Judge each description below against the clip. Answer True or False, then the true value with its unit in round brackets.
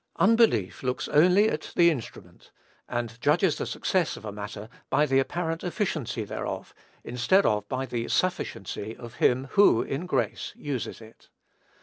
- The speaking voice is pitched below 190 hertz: True (135 Hz)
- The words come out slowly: False (155 wpm)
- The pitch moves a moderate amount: False (7.1 semitones)